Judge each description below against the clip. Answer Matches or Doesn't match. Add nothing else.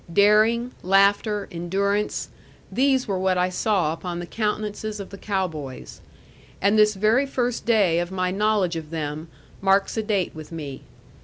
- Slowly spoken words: Doesn't match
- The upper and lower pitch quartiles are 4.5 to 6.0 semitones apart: Doesn't match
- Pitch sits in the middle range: Doesn't match